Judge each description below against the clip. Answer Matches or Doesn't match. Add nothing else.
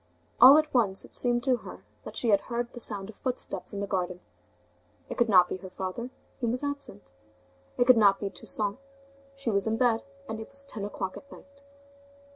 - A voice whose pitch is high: Matches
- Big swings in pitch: Doesn't match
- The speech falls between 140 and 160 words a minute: Doesn't match